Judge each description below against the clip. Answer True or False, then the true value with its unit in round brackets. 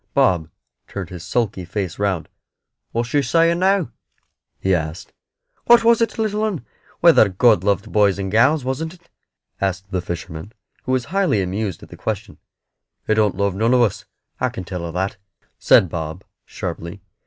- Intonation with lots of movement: True (6.4 semitones)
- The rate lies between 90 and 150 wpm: False (170 wpm)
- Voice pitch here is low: True (105 Hz)